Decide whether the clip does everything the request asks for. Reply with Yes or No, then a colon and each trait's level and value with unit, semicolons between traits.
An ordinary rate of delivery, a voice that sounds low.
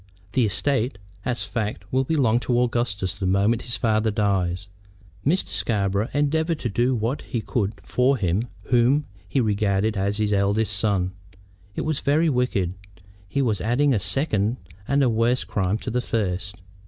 Yes: average, 165 wpm; low, 110 Hz